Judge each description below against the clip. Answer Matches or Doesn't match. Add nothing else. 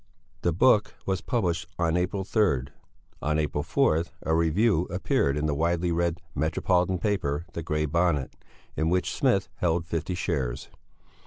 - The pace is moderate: Matches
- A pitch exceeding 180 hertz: Doesn't match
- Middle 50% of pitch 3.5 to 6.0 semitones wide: Doesn't match